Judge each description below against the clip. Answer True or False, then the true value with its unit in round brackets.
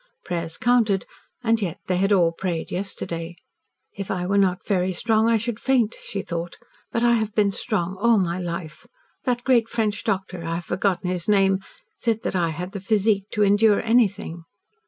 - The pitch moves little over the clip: False (3.7 semitones)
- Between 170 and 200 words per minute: True (185 wpm)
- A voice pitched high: True (195 Hz)